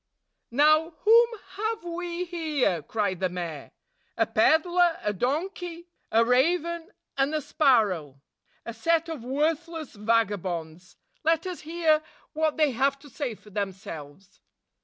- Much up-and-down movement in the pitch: Yes, wide, 8.2 semitones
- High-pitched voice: Yes, very high, 290 Hz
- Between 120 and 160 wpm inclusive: Yes, slow, 135 wpm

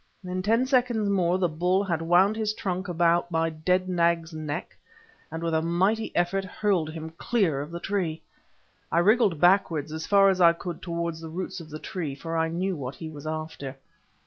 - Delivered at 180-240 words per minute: Yes, average, 200 wpm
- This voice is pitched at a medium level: Yes, medium, 170 Hz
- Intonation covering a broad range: No, average, 3.0 semitones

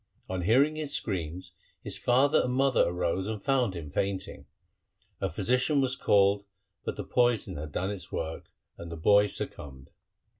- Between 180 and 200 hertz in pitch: No, low, 100 Hz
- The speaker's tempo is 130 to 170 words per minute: Yes, average, 160 wpm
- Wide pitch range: Yes, wide, 6.2 semitones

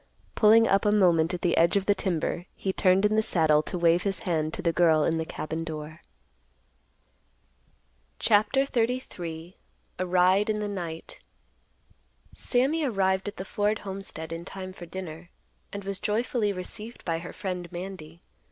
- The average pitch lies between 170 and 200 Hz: Yes, medium, 185 Hz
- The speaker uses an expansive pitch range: No, average, 3.7 semitones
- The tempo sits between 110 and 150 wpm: No, average, 165 wpm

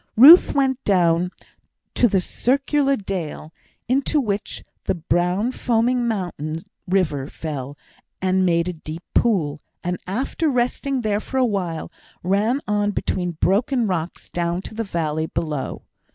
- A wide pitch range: Yes, wide, 6.1 semitones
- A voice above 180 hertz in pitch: Yes, high, 190 Hz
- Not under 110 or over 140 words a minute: Yes, slow, 135 wpm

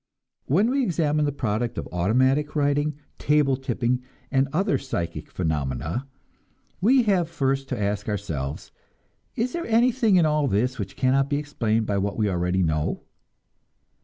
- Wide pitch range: Yes, wide, 6.9 semitones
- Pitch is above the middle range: No, low, 135 Hz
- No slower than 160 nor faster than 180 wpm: No, average, 150 wpm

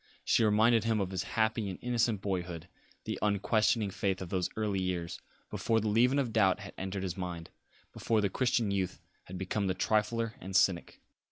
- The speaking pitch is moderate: No, low, 100 Hz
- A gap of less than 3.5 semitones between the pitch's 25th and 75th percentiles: Yes, average, 3.1 semitones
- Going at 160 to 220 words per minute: Yes, average, 185 wpm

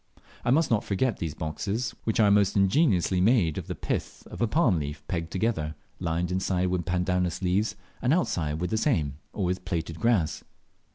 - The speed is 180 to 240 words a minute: Yes, average, 185 wpm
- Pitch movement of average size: Yes, average, 4.7 semitones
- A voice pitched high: No, very low, 90 Hz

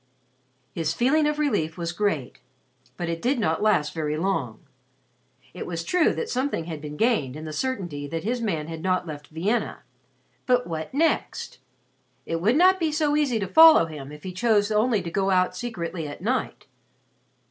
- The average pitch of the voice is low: No, medium, 185 Hz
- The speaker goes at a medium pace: Yes, average, 180 wpm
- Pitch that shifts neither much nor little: No, wide, 7.6 semitones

